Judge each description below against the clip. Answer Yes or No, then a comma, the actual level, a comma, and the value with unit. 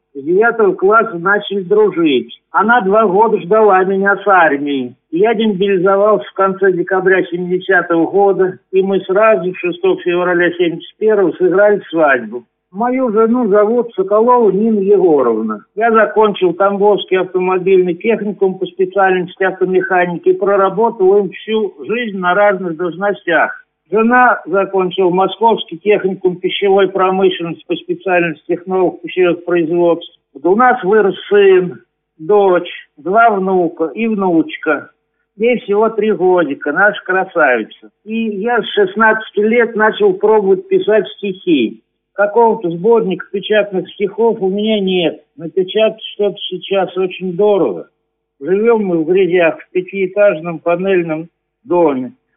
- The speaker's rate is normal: Yes, average, 120 wpm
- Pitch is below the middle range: No, high, 195 Hz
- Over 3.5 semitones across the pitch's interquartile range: No, average, 3.2 semitones